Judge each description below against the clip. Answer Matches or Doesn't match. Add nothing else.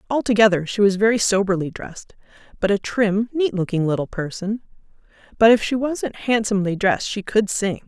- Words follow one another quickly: Doesn't match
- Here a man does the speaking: Doesn't match